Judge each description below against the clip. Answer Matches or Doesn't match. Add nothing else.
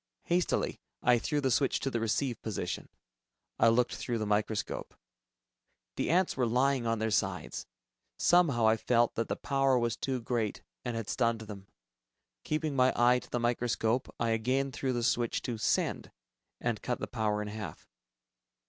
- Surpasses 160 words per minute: Matches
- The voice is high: Doesn't match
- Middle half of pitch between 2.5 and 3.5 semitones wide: Matches